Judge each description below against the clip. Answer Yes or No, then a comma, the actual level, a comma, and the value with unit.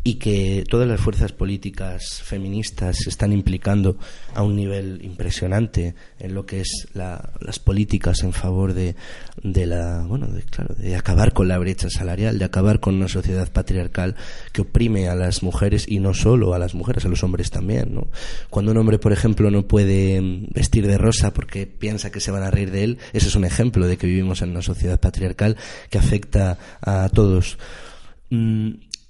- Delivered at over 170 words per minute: Yes, fast, 190 wpm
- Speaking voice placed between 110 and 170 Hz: No, very low, 95 Hz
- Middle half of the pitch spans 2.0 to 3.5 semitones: Yes, narrow, 2.5 semitones